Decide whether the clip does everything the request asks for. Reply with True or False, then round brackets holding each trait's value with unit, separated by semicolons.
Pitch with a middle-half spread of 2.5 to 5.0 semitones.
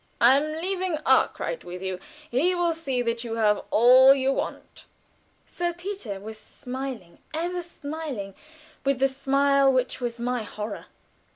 False (5.4 semitones)